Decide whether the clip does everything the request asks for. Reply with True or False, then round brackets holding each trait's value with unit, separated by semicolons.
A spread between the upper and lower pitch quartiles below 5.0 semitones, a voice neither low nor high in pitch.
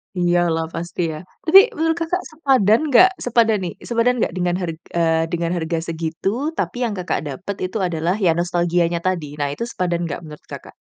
False (5.3 semitones; 175 Hz)